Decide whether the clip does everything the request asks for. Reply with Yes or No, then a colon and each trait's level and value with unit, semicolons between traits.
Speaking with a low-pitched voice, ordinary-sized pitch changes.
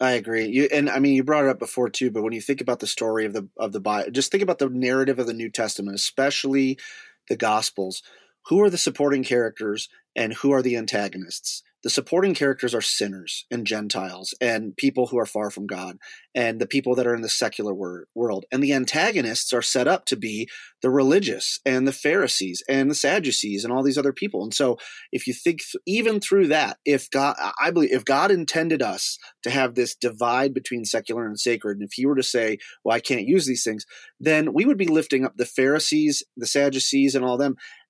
Yes: low, 125 Hz; average, 4.0 semitones